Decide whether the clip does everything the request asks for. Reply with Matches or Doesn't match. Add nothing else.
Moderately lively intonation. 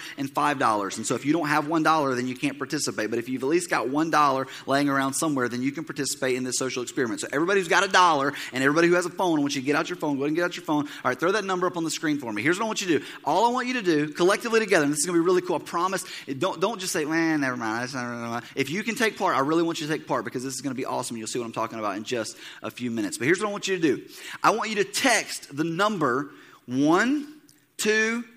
Doesn't match